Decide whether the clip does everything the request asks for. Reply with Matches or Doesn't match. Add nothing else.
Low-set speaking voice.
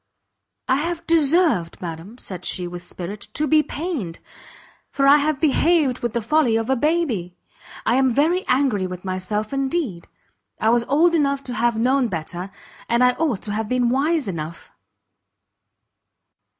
Doesn't match